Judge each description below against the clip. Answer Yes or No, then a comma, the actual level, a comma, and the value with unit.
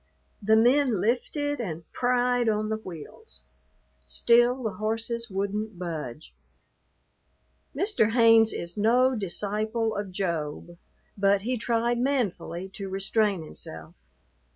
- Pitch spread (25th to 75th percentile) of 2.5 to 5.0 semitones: Yes, average, 3.9 semitones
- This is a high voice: Yes, high, 220 Hz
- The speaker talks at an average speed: No, slow, 110 wpm